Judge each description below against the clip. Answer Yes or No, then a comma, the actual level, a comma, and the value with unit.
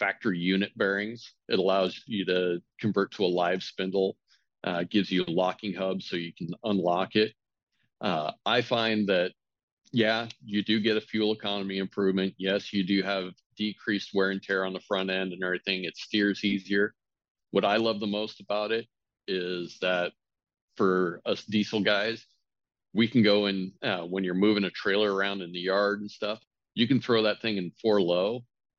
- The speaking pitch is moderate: No, low, 100 Hz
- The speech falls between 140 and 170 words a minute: No, average, 185 wpm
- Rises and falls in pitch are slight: Yes, narrow, 2.2 semitones